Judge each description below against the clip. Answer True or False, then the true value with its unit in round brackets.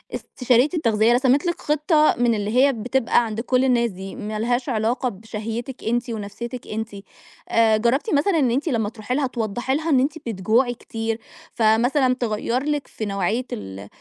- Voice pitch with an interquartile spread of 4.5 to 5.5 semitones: False (3.2 semitones)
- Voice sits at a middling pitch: False (240 Hz)